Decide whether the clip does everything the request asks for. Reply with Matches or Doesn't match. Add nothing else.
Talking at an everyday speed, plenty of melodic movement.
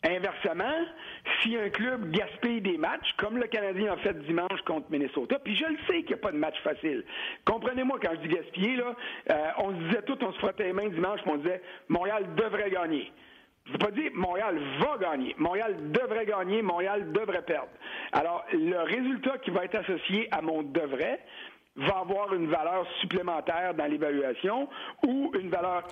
Matches